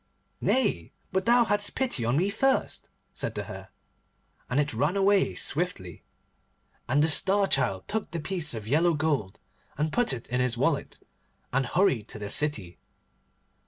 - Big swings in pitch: Yes, wide, 8.0 semitones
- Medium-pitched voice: Yes, medium, 150 Hz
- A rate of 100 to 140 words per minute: No, average, 160 wpm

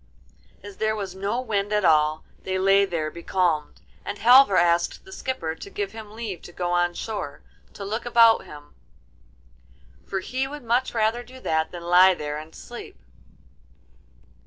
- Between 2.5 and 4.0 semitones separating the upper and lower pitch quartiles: No, average, 4.7 semitones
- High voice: Yes, high, 195 Hz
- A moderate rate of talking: Yes, average, 165 wpm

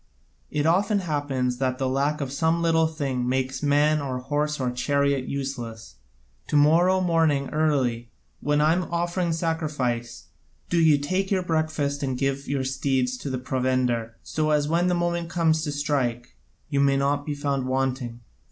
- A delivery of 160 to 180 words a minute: Yes, average, 165 wpm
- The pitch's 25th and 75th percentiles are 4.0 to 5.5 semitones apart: No, average, 3.5 semitones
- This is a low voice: No, medium, 145 Hz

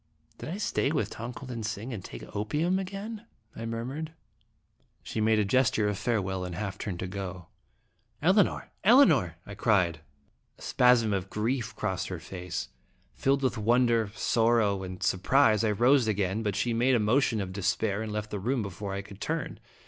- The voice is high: No, low, 110 Hz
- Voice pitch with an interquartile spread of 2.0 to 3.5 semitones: No, average, 4.2 semitones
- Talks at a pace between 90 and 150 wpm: No, average, 185 wpm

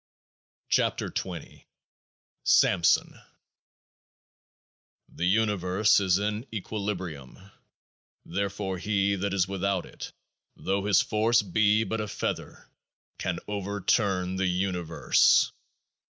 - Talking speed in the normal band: No, slow, 95 wpm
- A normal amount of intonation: No, narrow, 2.1 semitones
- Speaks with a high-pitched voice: No, low, 100 Hz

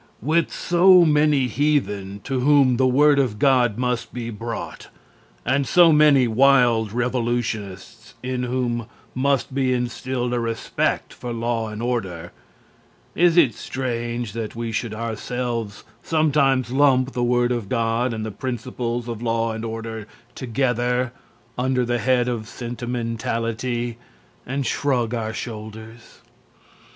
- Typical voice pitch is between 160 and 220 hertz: No, low, 120 Hz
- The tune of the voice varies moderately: No, narrow, 2.2 semitones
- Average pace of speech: No, slow, 130 wpm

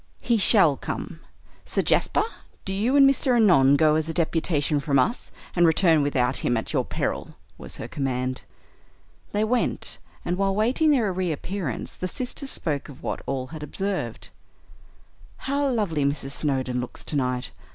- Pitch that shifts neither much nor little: No, wide, 7.2 semitones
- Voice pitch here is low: No, medium, 160 Hz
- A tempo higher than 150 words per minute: Yes, average, 160 wpm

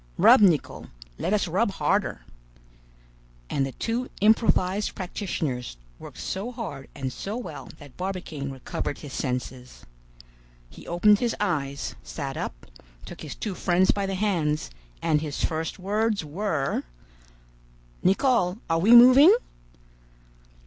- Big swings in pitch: Yes, wide, 6.5 semitones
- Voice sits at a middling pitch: Yes, medium, 180 Hz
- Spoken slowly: Yes, slow, 130 wpm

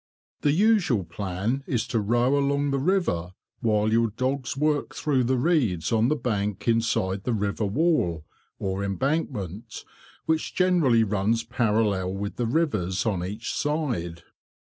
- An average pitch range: No, wide, 6.0 semitones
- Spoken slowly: No, average, 145 wpm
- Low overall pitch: Yes, low, 115 Hz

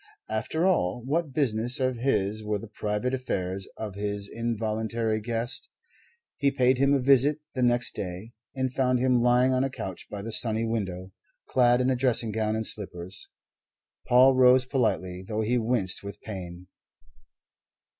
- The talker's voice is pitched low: Yes, low, 115 Hz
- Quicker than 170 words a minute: No, average, 155 wpm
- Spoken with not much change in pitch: No, average, 3.6 semitones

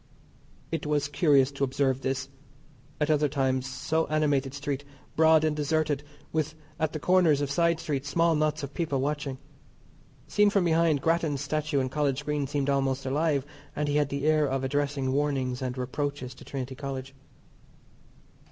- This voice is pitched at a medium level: Yes, medium, 145 Hz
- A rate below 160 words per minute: No, average, 165 wpm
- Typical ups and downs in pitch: No, narrow, 2.2 semitones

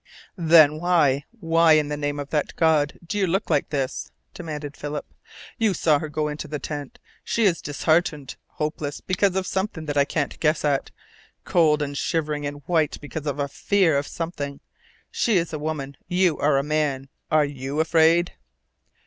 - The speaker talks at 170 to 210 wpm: Yes, average, 180 wpm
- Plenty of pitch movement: No, narrow, 2.5 semitones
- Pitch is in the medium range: Yes, medium, 155 Hz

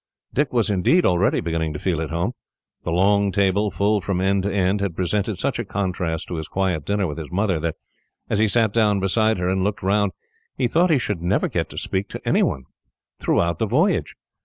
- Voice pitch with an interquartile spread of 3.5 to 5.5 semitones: No, average, 2.9 semitones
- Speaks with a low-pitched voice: Yes, very low, 95 Hz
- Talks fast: Yes, fast, 215 wpm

